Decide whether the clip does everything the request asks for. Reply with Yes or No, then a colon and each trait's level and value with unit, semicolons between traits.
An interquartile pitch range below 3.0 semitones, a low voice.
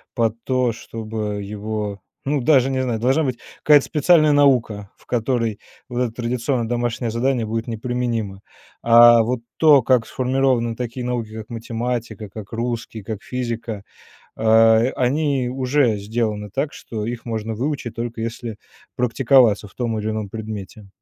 Yes: narrow, 2.4 semitones; low, 115 Hz